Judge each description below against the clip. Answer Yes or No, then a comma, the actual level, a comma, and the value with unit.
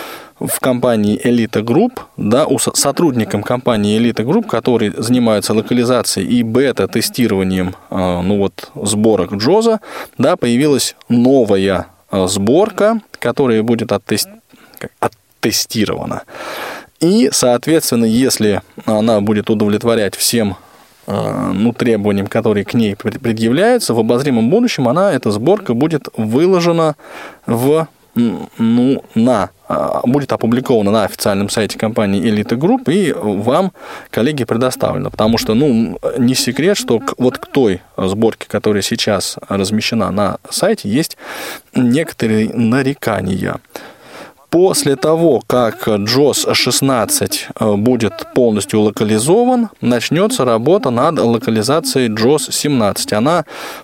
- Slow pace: Yes, slow, 105 wpm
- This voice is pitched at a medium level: No, low, 115 Hz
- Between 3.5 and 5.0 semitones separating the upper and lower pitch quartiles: Yes, average, 4.0 semitones